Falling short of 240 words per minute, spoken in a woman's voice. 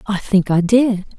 Yes: fast, 205 wpm; female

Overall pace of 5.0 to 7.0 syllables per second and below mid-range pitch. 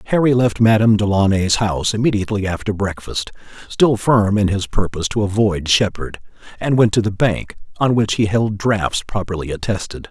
Yes: 5.4 syllables/s; low, 105 Hz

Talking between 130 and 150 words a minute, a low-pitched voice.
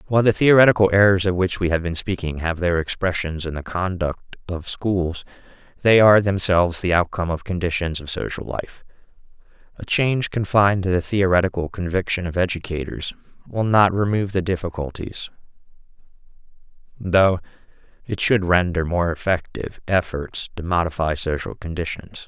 Yes: average, 145 wpm; very low, 90 Hz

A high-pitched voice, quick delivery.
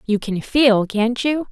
No: high, 235 Hz; average, 195 wpm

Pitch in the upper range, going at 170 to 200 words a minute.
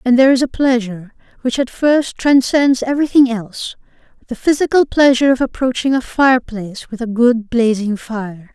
No: high, 245 Hz; average, 155 wpm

